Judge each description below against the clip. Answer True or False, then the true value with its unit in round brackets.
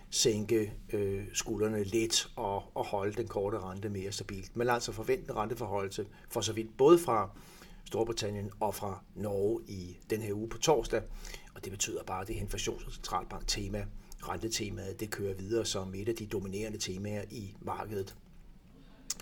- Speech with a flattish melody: True (2.2 semitones)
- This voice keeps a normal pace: True (160 wpm)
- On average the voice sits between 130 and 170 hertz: False (105 Hz)